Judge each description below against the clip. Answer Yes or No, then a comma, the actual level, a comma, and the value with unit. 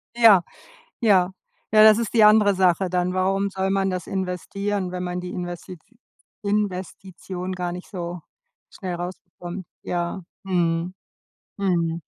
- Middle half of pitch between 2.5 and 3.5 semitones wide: No, narrow, 1.8 semitones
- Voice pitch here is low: No, medium, 185 Hz